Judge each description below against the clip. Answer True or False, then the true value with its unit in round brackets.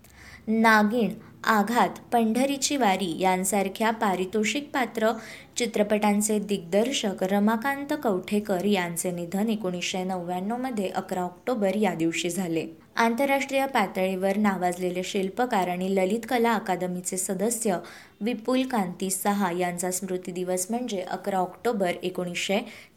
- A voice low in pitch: False (200 Hz)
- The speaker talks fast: False (105 wpm)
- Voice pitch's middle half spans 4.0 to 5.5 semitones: False (3.6 semitones)